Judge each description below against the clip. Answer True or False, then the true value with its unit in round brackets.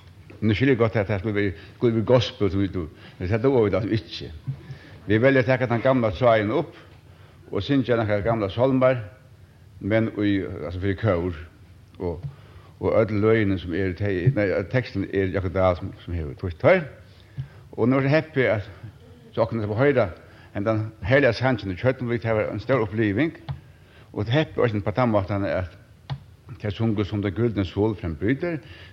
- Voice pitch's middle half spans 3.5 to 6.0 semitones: True (4.0 semitones)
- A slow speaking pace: False (190 wpm)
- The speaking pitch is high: False (105 Hz)